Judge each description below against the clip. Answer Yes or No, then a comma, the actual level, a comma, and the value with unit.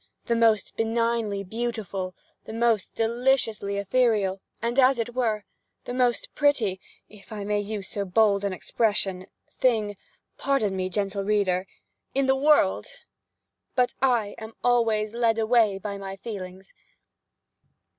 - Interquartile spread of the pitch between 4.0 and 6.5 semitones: No, average, 3.1 semitones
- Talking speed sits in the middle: No, slow, 130 wpm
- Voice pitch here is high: Yes, high, 215 Hz